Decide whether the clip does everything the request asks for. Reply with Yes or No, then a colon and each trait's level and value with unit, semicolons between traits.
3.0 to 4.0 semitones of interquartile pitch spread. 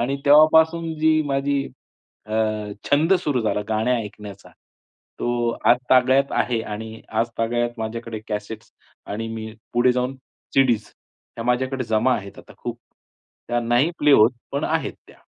Yes: average, 3.5 semitones